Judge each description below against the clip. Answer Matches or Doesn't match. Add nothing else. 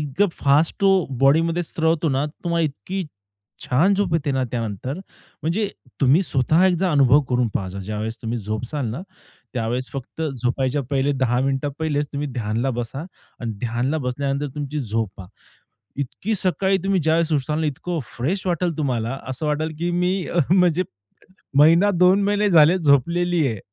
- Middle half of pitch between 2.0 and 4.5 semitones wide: Doesn't match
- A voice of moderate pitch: Matches